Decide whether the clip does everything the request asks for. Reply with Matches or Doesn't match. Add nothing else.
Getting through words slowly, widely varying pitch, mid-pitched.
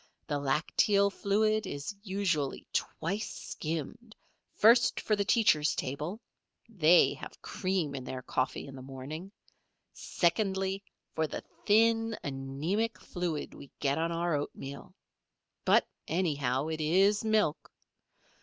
Matches